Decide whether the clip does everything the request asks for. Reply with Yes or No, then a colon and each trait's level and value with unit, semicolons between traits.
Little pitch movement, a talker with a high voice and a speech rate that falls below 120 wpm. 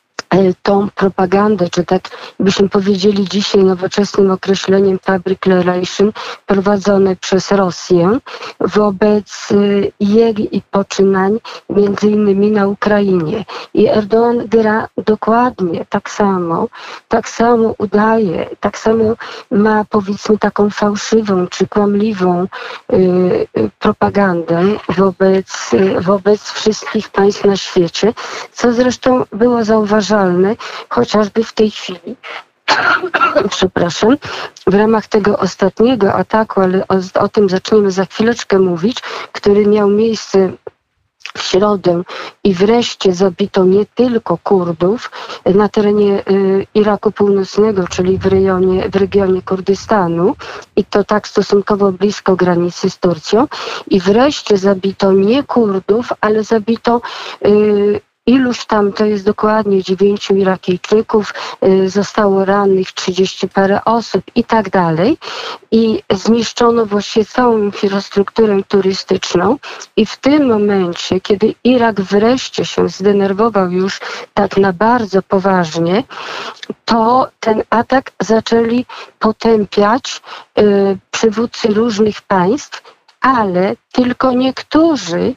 Yes: narrow, 2.3 semitones; high, 205 Hz; slow, 110 wpm